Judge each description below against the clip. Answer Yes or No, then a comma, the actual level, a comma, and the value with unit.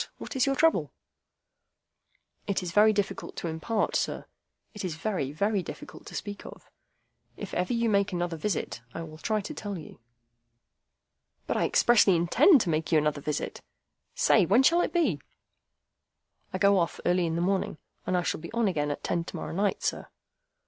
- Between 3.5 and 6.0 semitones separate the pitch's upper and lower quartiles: Yes, average, 4.5 semitones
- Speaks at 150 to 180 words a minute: No, average, 190 wpm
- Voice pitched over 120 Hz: Yes, high, 190 Hz